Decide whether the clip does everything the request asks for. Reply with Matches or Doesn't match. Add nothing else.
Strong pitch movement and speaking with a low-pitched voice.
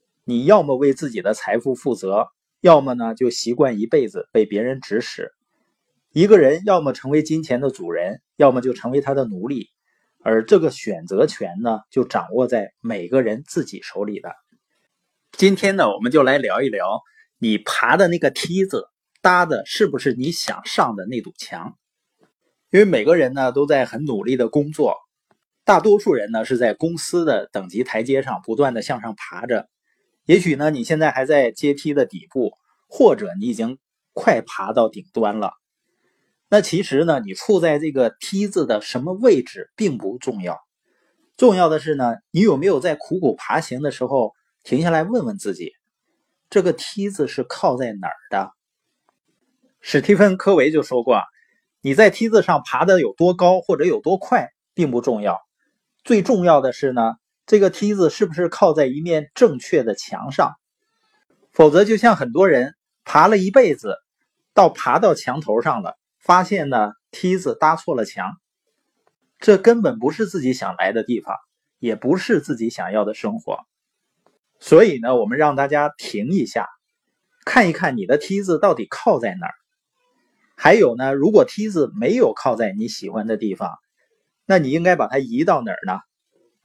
Doesn't match